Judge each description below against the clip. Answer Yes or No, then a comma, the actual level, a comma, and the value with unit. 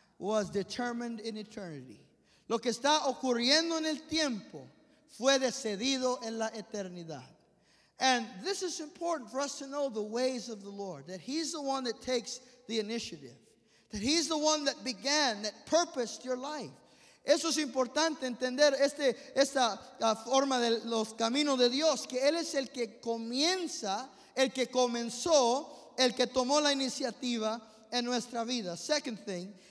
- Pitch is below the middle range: No, very high, 250 Hz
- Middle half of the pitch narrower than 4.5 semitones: Yes, average, 4.1 semitones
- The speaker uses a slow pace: No, average, 160 wpm